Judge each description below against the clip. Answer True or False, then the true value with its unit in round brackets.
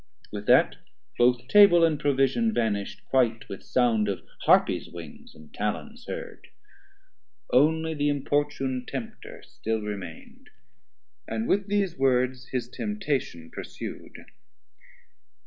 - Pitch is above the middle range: False (130 Hz)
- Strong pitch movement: False (4.9 semitones)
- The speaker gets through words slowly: True (115 wpm)